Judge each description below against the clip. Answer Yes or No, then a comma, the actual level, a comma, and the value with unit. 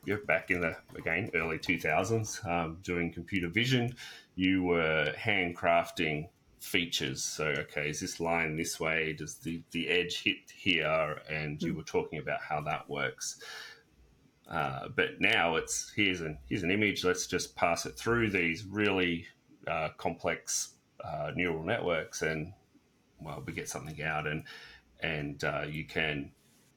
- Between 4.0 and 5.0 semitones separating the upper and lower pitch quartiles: No, average, 3.2 semitones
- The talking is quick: No, average, 155 wpm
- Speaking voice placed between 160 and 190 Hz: No, very low, 85 Hz